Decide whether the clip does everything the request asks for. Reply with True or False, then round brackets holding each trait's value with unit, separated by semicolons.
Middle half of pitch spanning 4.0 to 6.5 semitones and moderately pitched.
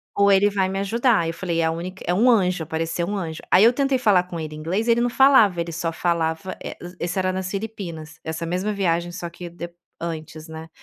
False (3.3 semitones; 180 Hz)